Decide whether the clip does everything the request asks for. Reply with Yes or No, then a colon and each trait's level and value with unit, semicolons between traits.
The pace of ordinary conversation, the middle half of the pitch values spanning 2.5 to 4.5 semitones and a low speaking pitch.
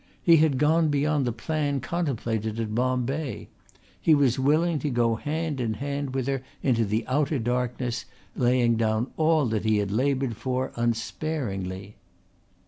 Yes: average, 150 wpm; average, 4.2 semitones; low, 130 Hz